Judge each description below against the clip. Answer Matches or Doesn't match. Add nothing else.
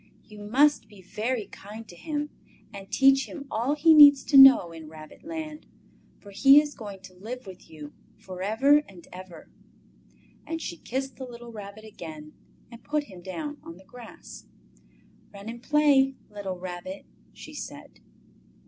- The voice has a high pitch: Matches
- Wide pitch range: Matches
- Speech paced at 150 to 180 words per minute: Matches